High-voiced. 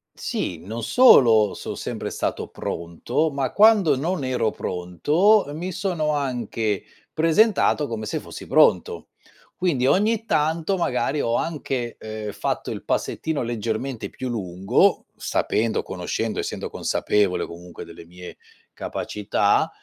No: low, 125 Hz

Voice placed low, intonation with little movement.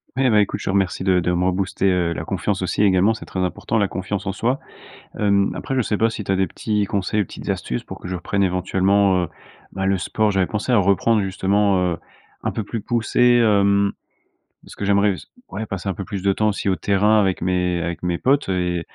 Yes: low, 100 Hz; narrow, 2.2 semitones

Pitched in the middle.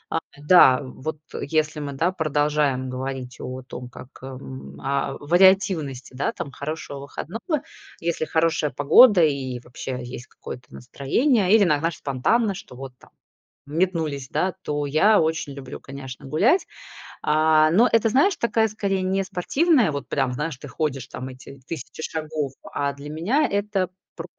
Yes: medium, 150 Hz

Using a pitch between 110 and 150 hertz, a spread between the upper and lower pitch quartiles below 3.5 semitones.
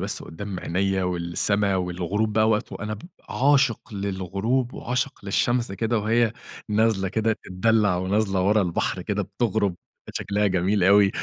No: low, 100 Hz; average, 2.7 semitones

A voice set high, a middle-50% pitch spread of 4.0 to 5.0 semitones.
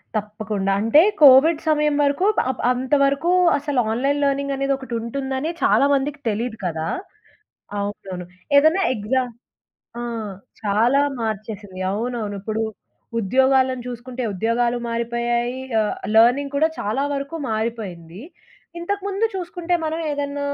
Yes: very high, 250 Hz; average, 4.4 semitones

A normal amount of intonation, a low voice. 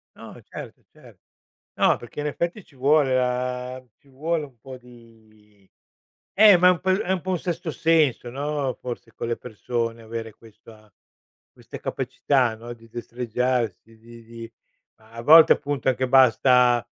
Yes: average, 3.9 semitones; low, 125 Hz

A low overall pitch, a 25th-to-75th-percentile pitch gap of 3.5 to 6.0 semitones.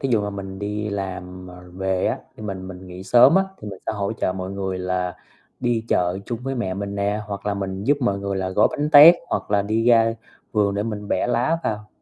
No: low, 100 Hz; average, 2.9 semitones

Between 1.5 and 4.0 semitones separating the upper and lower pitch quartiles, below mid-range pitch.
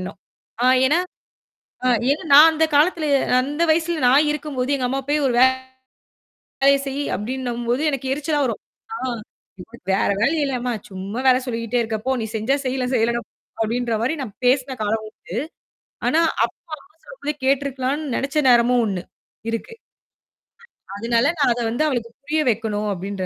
No: average, 3.6 semitones; very high, 255 Hz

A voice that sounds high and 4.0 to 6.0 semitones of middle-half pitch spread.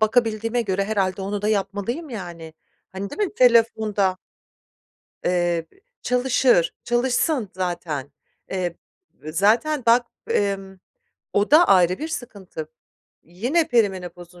Yes: high, 200 Hz; average, 4.9 semitones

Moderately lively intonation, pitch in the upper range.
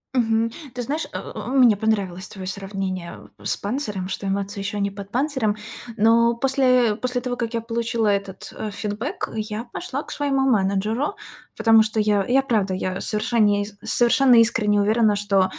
Yes: average, 3.4 semitones; high, 220 Hz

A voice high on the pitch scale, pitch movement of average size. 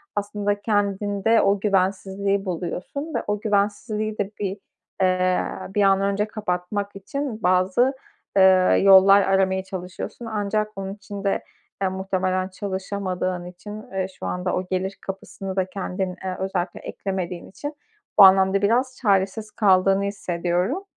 No: high, 195 Hz; narrow, 1.6 semitones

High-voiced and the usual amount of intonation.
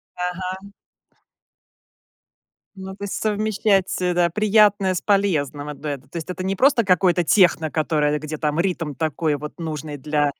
No: medium, 175 Hz; average, 4.3 semitones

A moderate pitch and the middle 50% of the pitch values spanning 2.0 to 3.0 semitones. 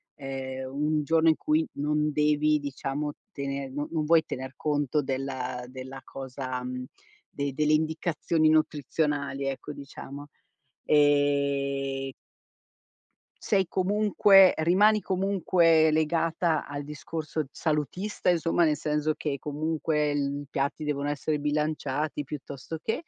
Yes: medium, 150 Hz; narrow, 2.3 semitones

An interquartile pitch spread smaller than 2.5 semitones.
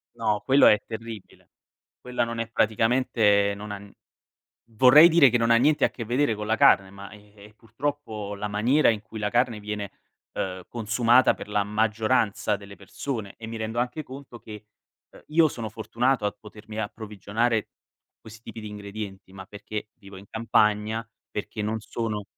Yes: narrow, 2.1 semitones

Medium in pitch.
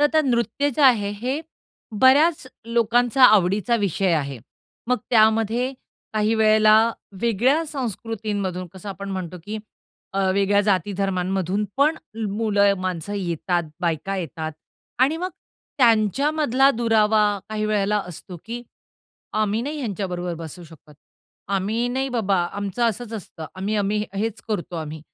No: high, 210 Hz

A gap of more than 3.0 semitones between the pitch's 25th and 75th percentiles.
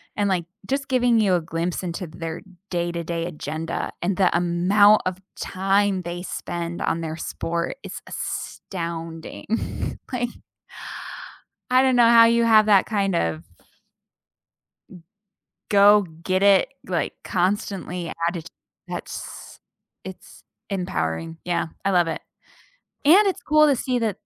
Yes: average, 3.9 semitones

